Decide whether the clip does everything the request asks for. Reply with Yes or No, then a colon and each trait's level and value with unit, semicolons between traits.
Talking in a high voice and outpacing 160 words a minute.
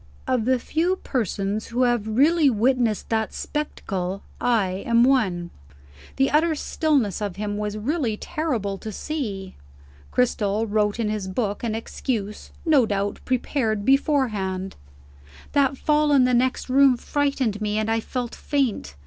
No: high, 230 Hz; average, 145 wpm